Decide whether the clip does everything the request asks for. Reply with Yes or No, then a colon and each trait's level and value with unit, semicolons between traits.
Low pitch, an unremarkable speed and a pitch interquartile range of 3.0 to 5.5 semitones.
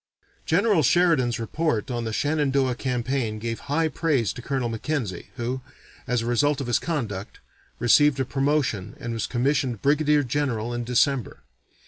Yes: low, 130 Hz; average, 150 wpm; average, 3.9 semitones